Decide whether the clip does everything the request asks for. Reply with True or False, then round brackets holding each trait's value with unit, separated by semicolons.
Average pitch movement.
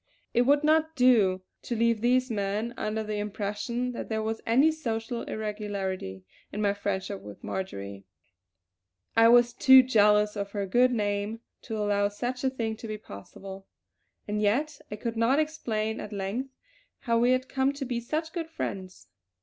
True (3.5 semitones)